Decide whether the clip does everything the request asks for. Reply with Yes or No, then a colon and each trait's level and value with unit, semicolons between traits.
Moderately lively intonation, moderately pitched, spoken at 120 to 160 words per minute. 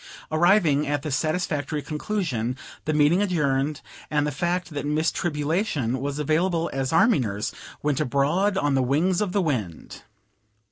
Yes: average, 3.8 semitones; medium, 150 Hz; average, 150 wpm